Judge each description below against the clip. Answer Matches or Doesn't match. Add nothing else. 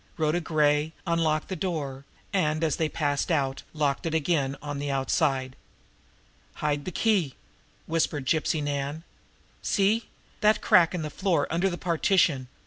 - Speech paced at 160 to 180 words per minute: Doesn't match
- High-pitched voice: Doesn't match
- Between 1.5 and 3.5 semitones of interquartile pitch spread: Matches